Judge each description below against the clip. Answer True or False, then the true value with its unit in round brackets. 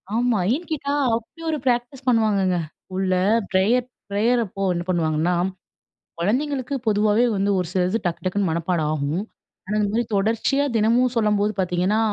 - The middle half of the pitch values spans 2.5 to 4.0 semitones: False (4.6 semitones)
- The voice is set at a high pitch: True (210 Hz)